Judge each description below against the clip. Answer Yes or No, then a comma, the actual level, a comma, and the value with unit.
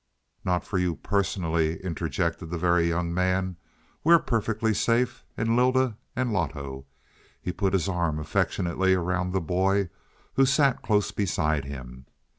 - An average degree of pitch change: Yes, average, 3.8 semitones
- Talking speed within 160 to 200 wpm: No, average, 140 wpm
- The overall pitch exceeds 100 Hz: No, very low, 90 Hz